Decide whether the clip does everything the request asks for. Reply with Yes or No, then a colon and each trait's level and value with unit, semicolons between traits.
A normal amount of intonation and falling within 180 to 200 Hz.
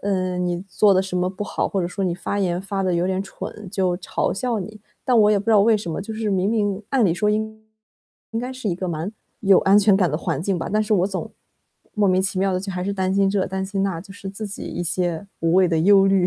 No: narrow, 2.2 semitones; high, 195 Hz